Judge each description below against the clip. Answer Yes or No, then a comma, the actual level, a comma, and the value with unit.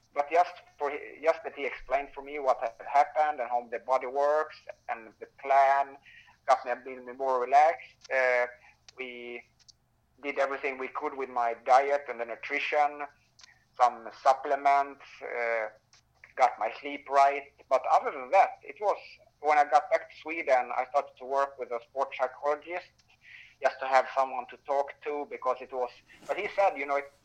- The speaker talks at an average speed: Yes, average, 180 wpm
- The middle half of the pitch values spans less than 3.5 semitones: Yes, narrow, 2.4 semitones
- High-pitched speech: No, medium, 140 Hz